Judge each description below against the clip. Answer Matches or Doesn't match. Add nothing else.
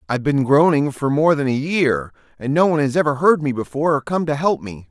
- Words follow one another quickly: Matches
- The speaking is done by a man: Matches